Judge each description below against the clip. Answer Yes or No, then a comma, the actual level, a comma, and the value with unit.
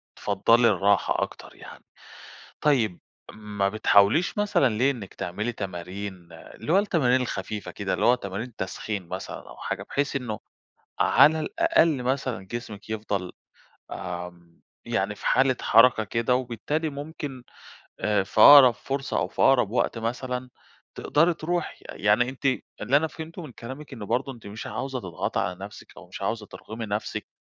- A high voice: No, low, 120 Hz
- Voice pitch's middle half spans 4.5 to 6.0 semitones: Yes, average, 5.2 semitones